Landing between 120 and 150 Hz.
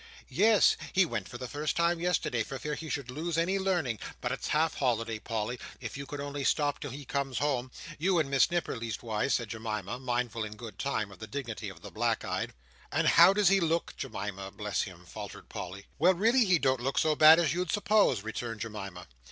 Yes: low, 135 Hz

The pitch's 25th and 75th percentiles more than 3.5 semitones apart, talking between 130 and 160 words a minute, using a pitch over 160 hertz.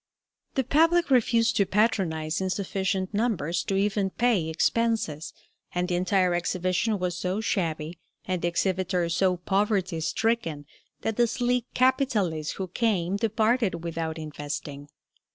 Yes: average, 4.7 semitones; slow, 135 wpm; high, 190 Hz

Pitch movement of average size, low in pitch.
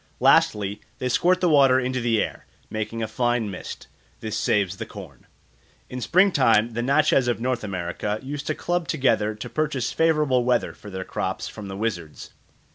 Yes: average, 4.7 semitones; low, 120 Hz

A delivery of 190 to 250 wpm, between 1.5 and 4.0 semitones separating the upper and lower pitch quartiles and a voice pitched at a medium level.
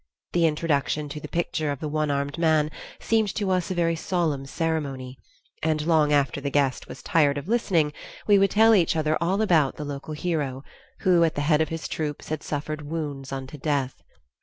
Yes: average, 200 wpm; average, 2.7 semitones; medium, 155 Hz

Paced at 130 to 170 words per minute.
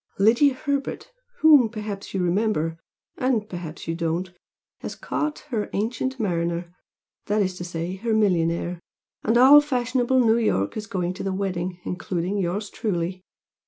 Yes: average, 150 wpm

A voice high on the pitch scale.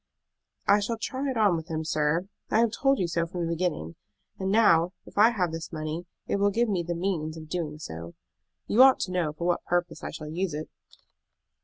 No: medium, 175 Hz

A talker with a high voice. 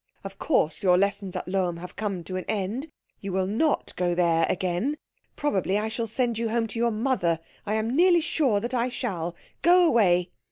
Yes: high, 210 Hz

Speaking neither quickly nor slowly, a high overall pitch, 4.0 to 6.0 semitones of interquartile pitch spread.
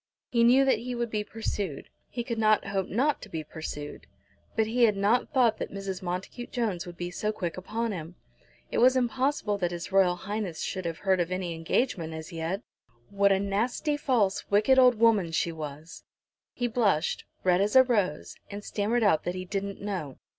Yes: average, 190 wpm; high, 200 Hz; average, 4.8 semitones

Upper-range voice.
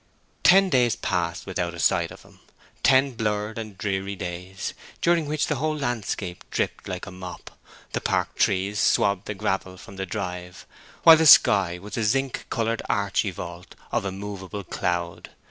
No: low, 100 Hz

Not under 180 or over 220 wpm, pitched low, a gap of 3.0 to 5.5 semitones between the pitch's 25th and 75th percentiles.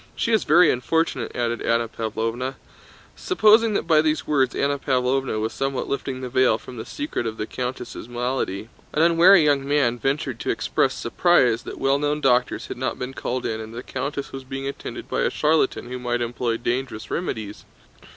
Yes: average, 190 wpm; low, 130 Hz; average, 3.6 semitones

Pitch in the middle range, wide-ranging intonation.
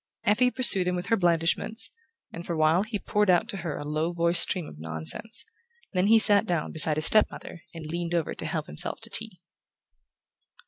No: medium, 175 Hz; average, 4.5 semitones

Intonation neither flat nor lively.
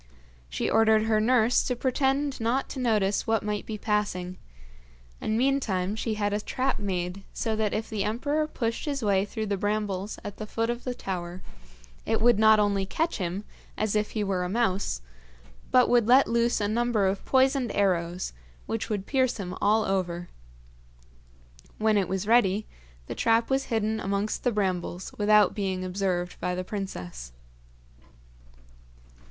Yes: average, 3.4 semitones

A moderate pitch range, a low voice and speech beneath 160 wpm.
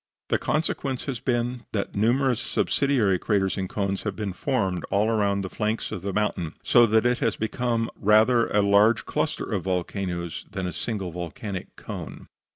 No: average, 3.5 semitones; low, 105 Hz; average, 165 wpm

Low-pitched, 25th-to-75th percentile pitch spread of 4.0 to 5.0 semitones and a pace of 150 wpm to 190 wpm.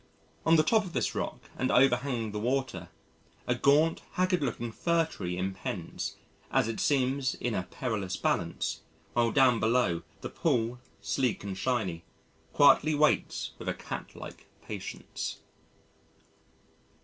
No: low, 125 Hz; average, 4.7 semitones; slow, 135 wpm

